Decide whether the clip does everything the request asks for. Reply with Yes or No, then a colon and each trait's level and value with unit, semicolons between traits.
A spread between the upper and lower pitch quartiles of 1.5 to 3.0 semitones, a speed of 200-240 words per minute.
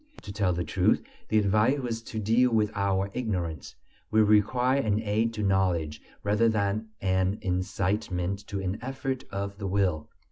No: average, 2.7 semitones; average, 165 wpm